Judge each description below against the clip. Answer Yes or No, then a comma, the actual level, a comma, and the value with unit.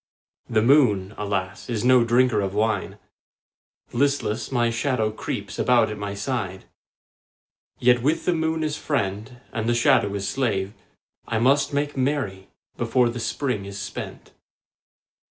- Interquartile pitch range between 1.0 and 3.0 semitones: No, average, 4.3 semitones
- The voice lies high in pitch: No, low, 115 Hz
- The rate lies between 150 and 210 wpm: No, average, 140 wpm